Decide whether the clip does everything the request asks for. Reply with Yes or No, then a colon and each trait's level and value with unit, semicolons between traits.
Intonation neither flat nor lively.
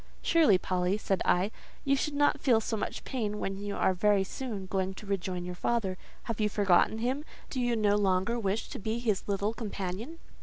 Yes: average, 3.4 semitones